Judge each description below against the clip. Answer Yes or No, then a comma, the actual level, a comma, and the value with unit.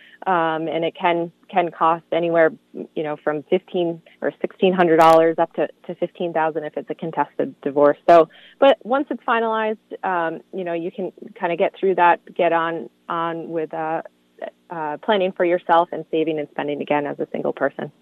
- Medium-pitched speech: Yes, medium, 165 Hz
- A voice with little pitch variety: Yes, narrow, 2.1 semitones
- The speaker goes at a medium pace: Yes, average, 195 wpm